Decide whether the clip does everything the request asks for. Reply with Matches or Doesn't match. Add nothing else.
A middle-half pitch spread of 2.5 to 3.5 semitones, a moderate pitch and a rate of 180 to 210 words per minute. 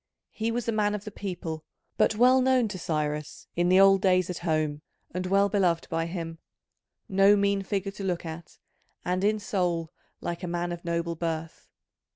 Matches